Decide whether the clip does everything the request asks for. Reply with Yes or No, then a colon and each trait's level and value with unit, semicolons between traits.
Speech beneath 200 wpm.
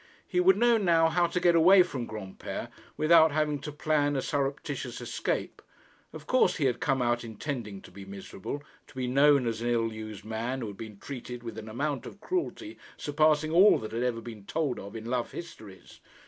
No: fast, 205 wpm